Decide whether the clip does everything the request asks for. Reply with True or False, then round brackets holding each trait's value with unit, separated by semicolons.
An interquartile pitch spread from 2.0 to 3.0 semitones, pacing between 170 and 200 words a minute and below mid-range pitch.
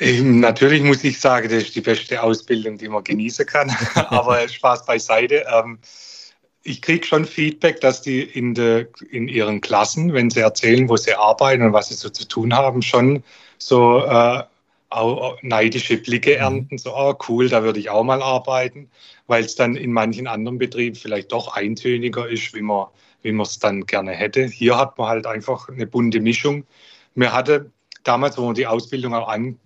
True (2.7 semitones; 185 wpm; 120 Hz)